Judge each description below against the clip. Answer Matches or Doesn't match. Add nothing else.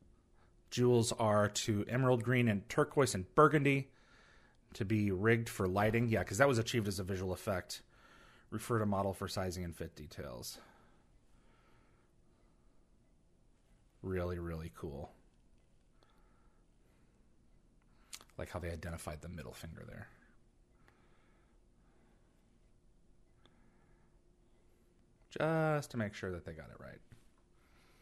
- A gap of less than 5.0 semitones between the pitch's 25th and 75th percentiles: Doesn't match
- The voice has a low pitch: Matches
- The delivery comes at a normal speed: Doesn't match